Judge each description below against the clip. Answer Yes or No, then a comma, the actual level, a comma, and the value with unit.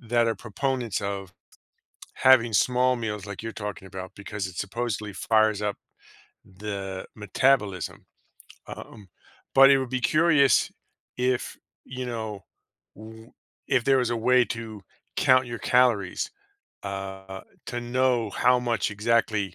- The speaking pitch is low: Yes, low, 115 Hz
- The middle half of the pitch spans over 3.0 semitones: Yes, average, 3.8 semitones